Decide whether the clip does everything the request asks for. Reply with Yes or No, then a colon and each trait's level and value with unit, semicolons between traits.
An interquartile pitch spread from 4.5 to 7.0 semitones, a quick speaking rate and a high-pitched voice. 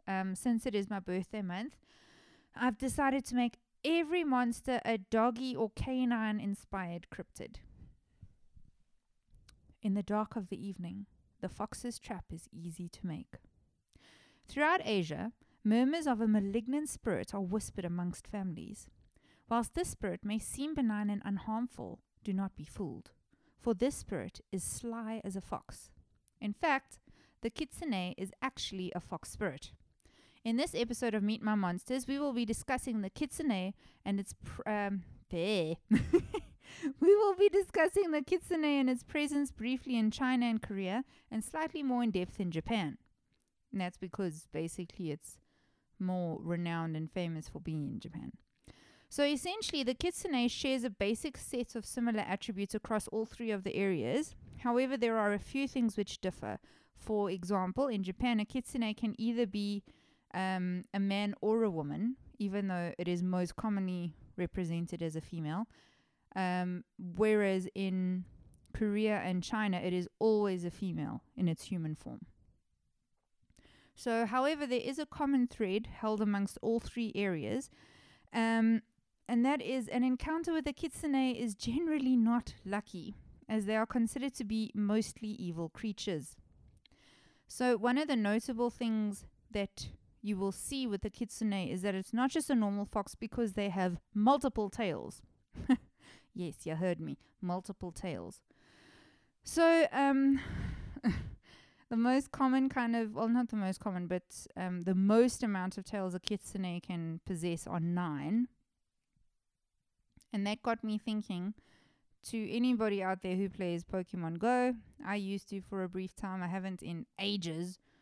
No: average, 4.8 semitones; average, 155 wpm; high, 215 Hz